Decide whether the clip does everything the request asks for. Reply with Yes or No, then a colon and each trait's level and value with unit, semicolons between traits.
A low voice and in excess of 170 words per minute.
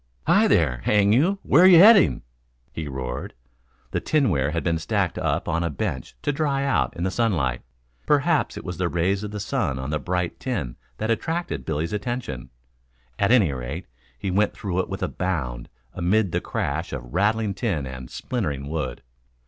Yes: very low, 90 Hz; average, 180 wpm